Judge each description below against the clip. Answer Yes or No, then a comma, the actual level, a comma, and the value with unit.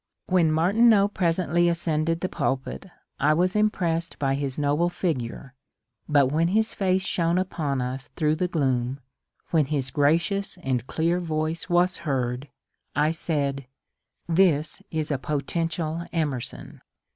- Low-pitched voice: No, medium, 160 Hz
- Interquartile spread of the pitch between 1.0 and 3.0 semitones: No, average, 3.7 semitones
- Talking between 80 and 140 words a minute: Yes, slow, 135 wpm